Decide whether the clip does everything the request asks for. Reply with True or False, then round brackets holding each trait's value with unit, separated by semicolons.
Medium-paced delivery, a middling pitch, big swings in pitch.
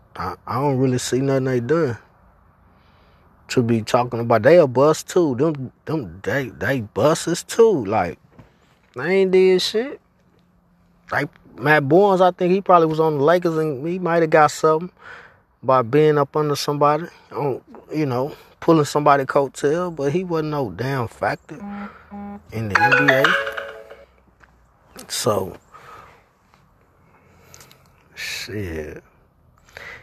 False (130 wpm; 145 Hz; 5.7 semitones)